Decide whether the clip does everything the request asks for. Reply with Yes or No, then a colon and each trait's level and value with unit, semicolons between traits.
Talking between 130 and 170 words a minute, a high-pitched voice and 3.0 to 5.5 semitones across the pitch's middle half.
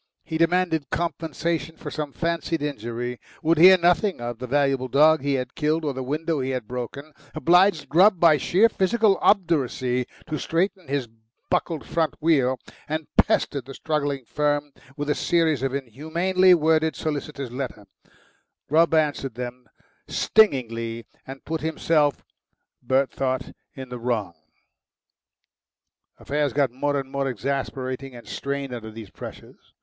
No: average, 145 wpm; medium, 145 Hz; average, 3.9 semitones